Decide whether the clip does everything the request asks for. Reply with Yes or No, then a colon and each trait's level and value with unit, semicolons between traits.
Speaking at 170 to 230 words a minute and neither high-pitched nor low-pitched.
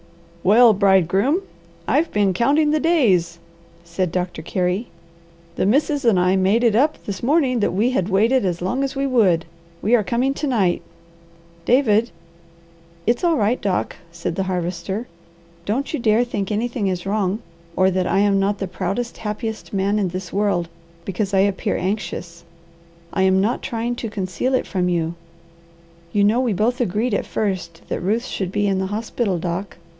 No: average, 175 wpm; high, 205 Hz